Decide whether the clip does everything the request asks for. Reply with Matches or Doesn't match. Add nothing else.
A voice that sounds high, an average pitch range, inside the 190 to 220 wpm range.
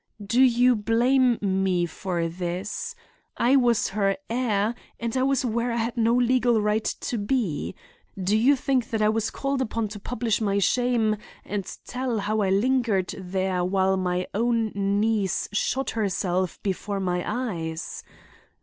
Doesn't match